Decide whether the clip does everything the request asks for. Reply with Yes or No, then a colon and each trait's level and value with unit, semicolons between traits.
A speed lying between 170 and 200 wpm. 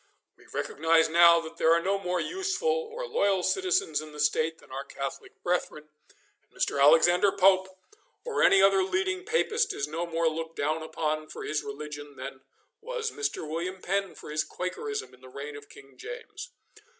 Yes: average, 180 wpm